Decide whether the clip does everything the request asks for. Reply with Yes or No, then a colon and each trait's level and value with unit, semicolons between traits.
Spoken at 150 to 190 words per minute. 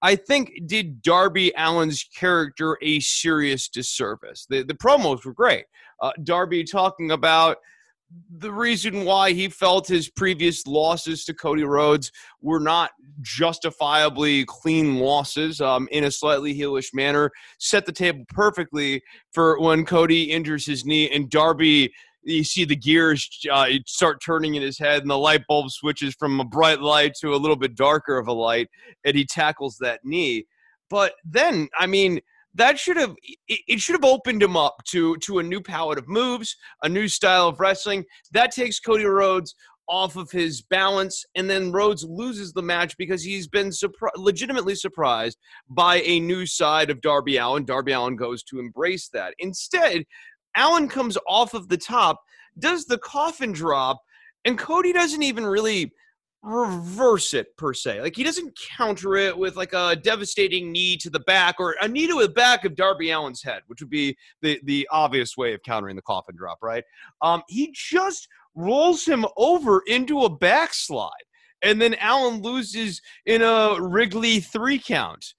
Yes: average, 170 wpm